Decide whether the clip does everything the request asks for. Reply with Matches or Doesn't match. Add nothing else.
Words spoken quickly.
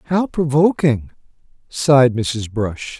Doesn't match